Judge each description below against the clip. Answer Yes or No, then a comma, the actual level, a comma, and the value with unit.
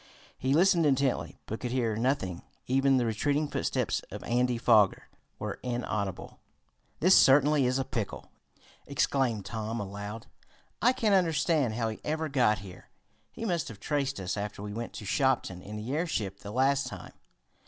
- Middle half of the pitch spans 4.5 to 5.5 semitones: Yes, average, 4.8 semitones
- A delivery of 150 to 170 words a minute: Yes, average, 165 wpm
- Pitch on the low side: Yes, low, 125 Hz